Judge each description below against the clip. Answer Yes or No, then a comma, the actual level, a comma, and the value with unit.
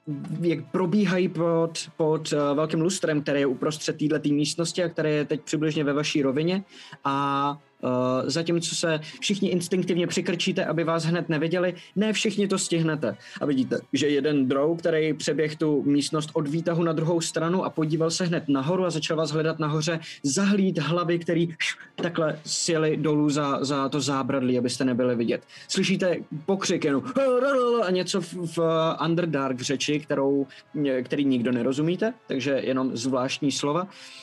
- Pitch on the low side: No, medium, 160 Hz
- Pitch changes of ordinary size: Yes, average, 3.3 semitones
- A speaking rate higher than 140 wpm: Yes, average, 155 wpm